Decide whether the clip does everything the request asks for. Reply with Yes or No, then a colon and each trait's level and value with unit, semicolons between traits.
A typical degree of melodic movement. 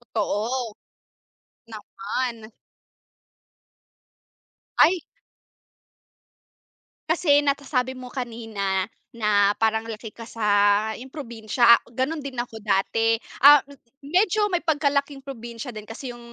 Yes: average, 4.1 semitones